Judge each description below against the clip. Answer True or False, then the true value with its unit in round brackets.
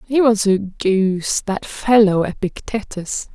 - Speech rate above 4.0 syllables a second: False (3.8 syllables/s)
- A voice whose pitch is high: True (205 Hz)